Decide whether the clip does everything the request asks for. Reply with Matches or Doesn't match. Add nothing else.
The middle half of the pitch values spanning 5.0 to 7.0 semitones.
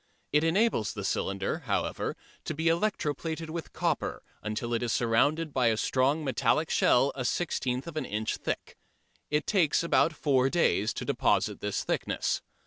Matches